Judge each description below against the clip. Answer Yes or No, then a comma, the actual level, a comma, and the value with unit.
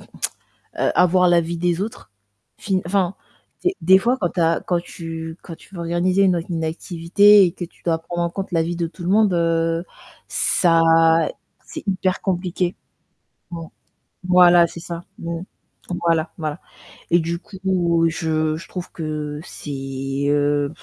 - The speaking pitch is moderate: Yes, medium, 170 Hz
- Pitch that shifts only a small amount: Yes, narrow, 1.9 semitones